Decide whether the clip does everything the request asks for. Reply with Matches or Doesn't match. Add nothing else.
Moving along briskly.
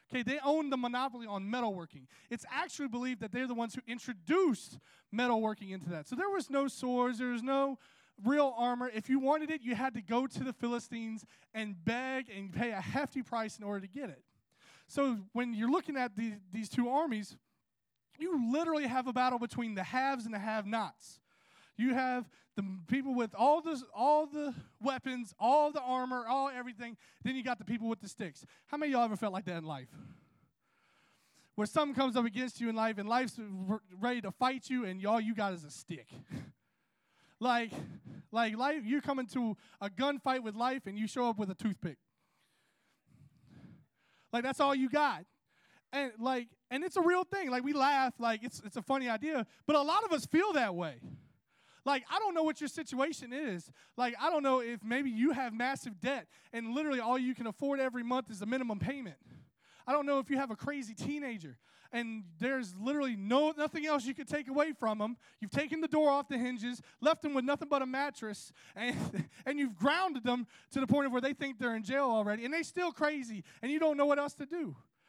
Matches